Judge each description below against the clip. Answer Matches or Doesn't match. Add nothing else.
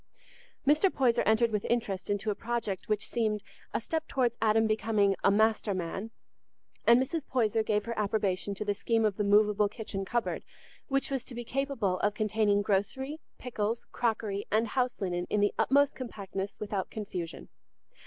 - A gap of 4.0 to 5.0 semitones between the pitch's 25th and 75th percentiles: Doesn't match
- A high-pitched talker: Matches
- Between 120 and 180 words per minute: Matches